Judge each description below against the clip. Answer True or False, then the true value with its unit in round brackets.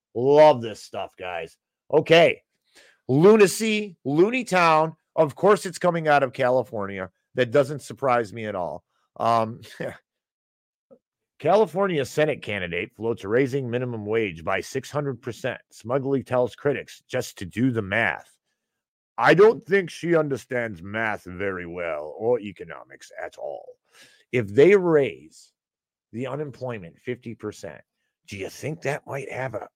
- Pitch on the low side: True (130 Hz)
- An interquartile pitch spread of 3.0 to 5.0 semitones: False (5.6 semitones)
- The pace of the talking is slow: True (130 wpm)